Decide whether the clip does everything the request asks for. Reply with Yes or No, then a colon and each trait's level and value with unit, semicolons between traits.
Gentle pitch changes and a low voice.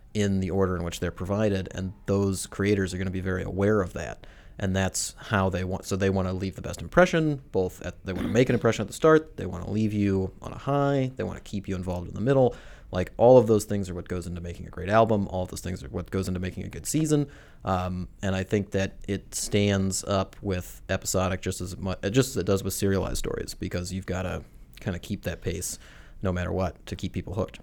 Yes: narrow, 2.0 semitones; very low, 95 Hz